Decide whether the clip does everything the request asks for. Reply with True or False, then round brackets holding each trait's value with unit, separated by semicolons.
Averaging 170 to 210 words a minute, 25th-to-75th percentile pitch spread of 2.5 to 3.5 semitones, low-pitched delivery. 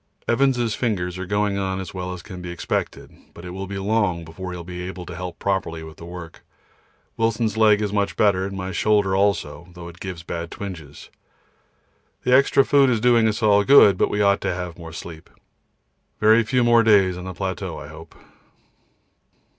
True (195 wpm; 3.2 semitones; 95 Hz)